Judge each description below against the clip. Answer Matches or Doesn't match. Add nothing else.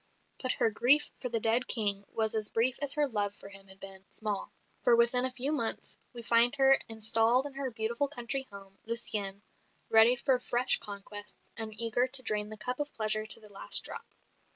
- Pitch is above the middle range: Matches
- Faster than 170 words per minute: Matches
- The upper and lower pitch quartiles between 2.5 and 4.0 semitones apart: Matches